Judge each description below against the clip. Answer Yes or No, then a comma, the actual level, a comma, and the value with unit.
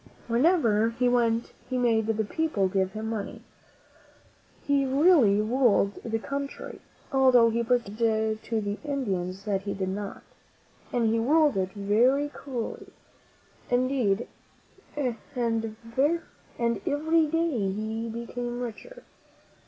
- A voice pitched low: No, high, 230 Hz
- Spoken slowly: Yes, slow, 120 wpm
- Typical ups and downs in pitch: Yes, average, 3.9 semitones